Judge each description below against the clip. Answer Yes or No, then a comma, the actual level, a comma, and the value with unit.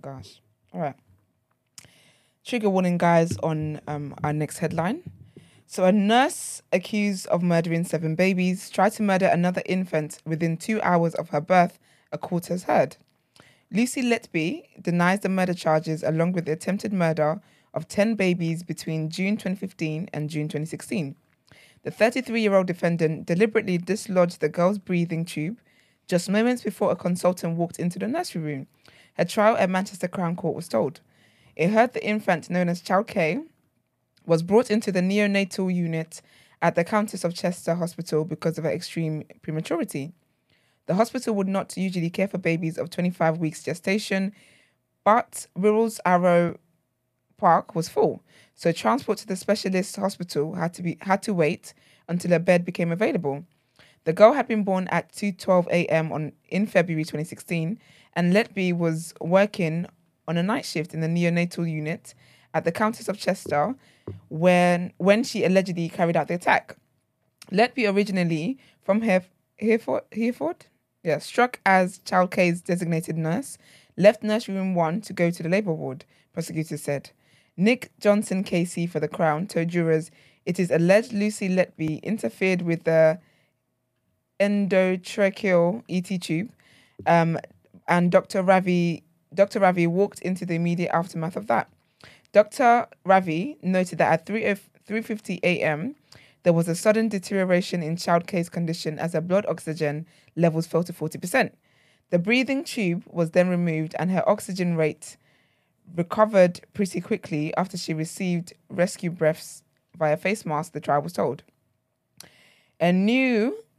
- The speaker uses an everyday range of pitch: Yes, average, 3.4 semitones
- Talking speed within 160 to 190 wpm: No, average, 150 wpm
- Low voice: No, medium, 175 Hz